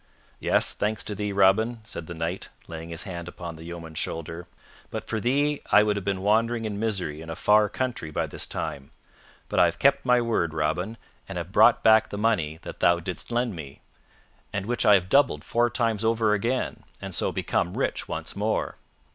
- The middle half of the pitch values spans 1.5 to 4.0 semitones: No, average, 5.2 semitones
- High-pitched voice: No, low, 100 Hz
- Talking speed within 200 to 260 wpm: Yes, fast, 205 wpm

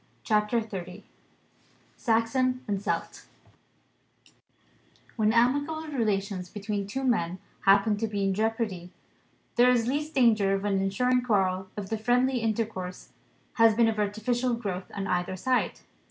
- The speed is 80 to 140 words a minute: Yes, slow, 135 wpm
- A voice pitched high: Yes, high, 215 Hz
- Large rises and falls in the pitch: No, average, 3.7 semitones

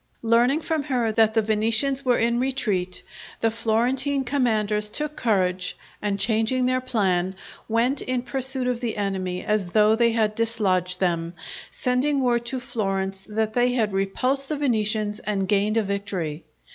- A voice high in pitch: Yes, high, 225 Hz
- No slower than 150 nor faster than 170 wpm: Yes, average, 160 wpm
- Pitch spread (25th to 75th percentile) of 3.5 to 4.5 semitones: Yes, average, 4.0 semitones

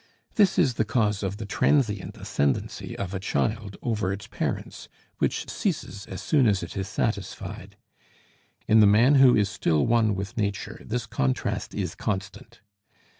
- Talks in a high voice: No, low, 105 Hz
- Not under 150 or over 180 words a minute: Yes, average, 160 wpm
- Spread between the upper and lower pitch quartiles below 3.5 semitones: Yes, average, 2.9 semitones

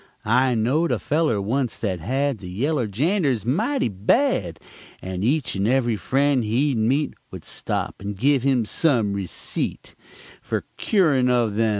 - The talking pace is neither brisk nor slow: Yes, average, 155 wpm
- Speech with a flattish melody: No, average, 5.2 semitones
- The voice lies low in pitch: Yes, low, 125 Hz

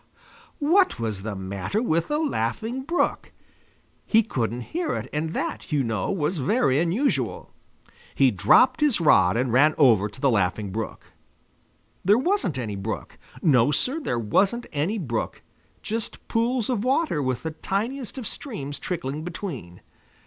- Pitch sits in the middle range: Yes, medium, 150 Hz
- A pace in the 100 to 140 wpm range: No, average, 150 wpm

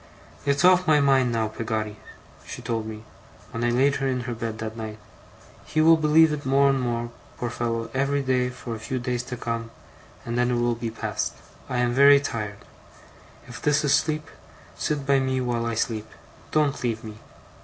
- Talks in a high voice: No, low, 125 Hz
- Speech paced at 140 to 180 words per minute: No, average, 195 wpm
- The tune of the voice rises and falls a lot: No, average, 3.3 semitones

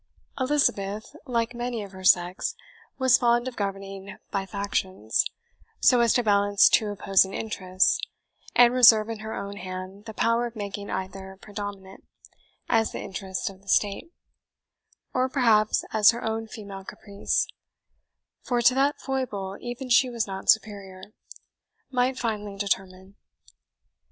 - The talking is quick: No, average, 140 wpm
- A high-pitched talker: Yes, high, 210 Hz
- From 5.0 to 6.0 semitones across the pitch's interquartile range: No, average, 3.4 semitones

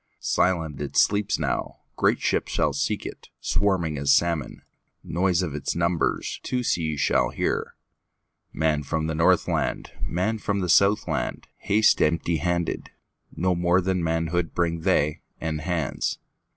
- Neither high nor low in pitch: No, very low, 85 Hz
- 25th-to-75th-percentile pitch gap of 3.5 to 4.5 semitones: No, narrow, 2.6 semitones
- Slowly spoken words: Yes, slow, 110 wpm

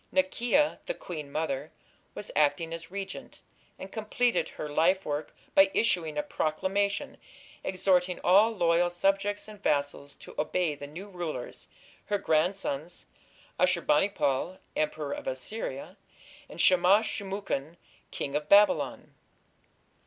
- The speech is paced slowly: Yes, slow, 125 wpm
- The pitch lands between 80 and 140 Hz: No, medium, 175 Hz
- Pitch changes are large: No, average, 4.7 semitones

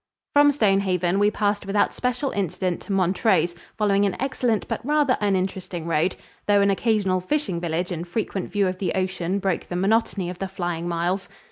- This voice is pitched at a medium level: No, high, 195 Hz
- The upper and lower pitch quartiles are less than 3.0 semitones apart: Yes, narrow, 2.6 semitones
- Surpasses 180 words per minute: No, average, 175 wpm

